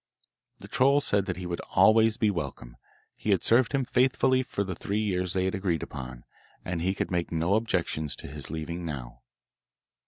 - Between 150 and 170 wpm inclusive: No, average, 190 wpm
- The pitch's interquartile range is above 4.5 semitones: Yes, average, 5.3 semitones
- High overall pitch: No, very low, 90 Hz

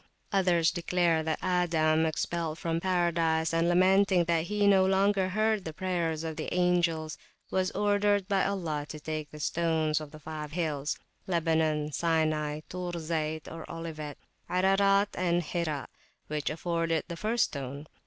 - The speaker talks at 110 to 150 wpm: Yes, average, 145 wpm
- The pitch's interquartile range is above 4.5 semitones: No, average, 2.8 semitones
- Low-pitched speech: No, medium, 165 Hz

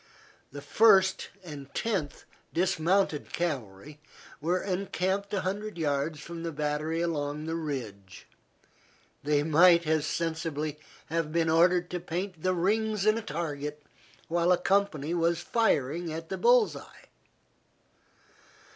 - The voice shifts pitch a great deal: No, average, 3.6 semitones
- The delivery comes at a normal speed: No, slow, 130 wpm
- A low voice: No, medium, 165 Hz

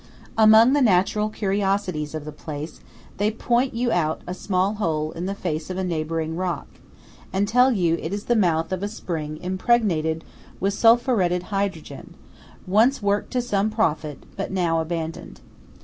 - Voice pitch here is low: No, medium, 185 Hz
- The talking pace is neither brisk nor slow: Yes, average, 165 wpm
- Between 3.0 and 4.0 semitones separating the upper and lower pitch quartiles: No, average, 4.8 semitones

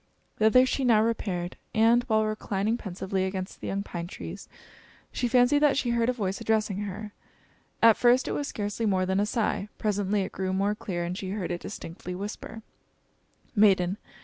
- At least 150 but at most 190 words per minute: Yes, average, 180 wpm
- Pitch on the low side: No, high, 205 Hz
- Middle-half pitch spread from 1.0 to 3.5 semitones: Yes, average, 3.1 semitones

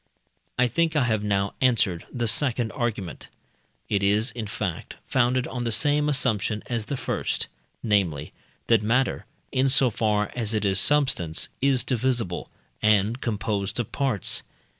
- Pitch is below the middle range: Yes, low, 115 Hz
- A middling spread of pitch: Yes, average, 3.8 semitones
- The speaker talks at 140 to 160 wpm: Yes, average, 150 wpm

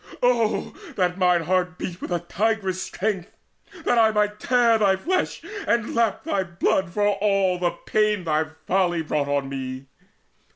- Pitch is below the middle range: No, high, 190 Hz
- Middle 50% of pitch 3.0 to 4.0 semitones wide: Yes, average, 3.5 semitones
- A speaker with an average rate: Yes, average, 160 wpm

